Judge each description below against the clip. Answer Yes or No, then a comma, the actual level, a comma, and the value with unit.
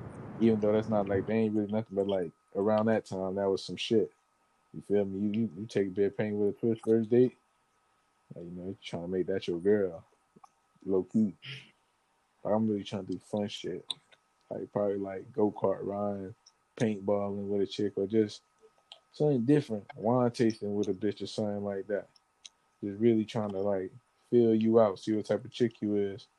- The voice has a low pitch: Yes, low, 105 Hz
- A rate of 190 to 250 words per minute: Yes, fast, 205 wpm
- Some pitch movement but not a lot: No, narrow, 2.3 semitones